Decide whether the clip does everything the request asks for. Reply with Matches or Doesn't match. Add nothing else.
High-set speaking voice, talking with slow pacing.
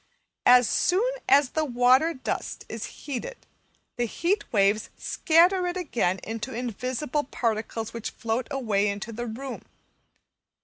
Matches